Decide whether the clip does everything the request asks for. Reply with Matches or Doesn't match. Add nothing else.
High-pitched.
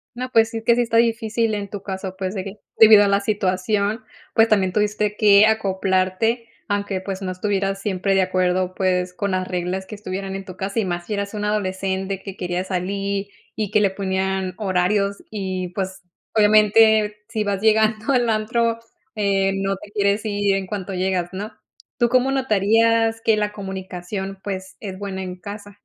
Matches